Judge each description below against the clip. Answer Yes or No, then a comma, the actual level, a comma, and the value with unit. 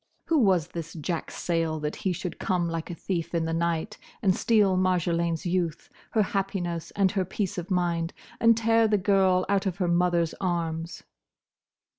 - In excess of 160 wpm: Yes, average, 175 wpm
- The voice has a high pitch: No, medium, 180 Hz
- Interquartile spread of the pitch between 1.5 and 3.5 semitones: Yes, narrow, 2.5 semitones